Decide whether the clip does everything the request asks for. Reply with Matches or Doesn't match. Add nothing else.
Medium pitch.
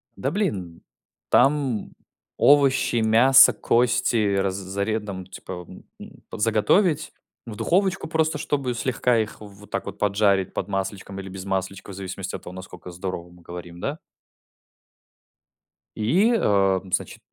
Doesn't match